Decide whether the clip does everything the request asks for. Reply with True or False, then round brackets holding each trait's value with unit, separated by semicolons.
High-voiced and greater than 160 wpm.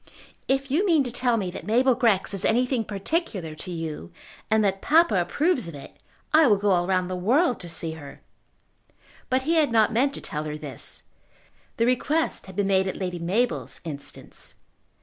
True (210 Hz; 190 wpm)